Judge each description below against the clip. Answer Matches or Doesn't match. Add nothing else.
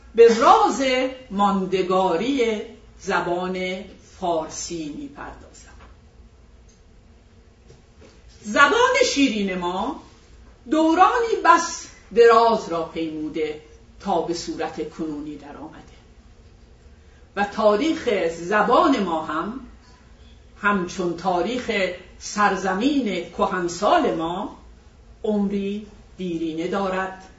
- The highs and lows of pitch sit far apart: Matches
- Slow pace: Matches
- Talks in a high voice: Matches